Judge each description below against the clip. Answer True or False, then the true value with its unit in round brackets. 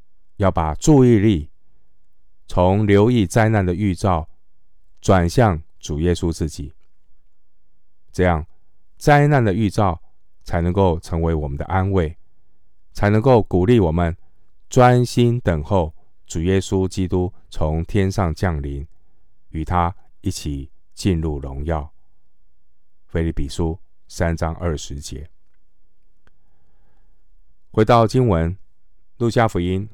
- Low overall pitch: True (90 Hz)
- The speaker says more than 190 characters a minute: False (165 characters per minute)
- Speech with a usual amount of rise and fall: True (4.1 semitones)